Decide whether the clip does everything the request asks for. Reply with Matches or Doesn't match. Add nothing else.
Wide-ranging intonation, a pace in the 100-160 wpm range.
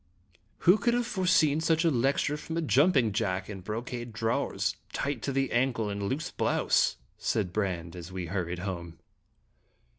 Doesn't match